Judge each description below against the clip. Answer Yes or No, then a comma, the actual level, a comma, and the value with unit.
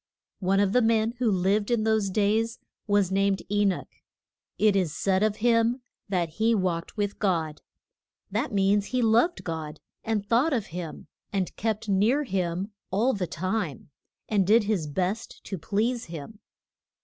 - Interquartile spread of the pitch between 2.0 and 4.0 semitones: Yes, average, 3.1 semitones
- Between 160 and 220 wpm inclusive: Yes, average, 165 wpm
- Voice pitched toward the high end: Yes, high, 205 Hz